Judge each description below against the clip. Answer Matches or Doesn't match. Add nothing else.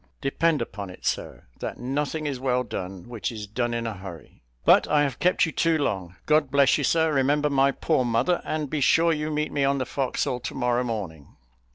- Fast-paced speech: Matches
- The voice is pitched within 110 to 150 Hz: Matches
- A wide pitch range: Doesn't match